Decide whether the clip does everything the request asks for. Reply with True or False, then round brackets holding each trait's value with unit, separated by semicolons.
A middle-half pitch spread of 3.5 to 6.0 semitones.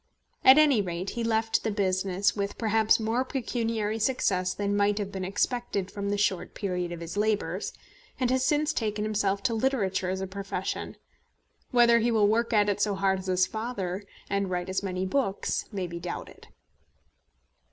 False (3.0 semitones)